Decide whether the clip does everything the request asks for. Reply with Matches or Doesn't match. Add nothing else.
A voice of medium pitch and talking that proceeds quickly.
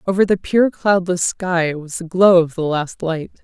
Matches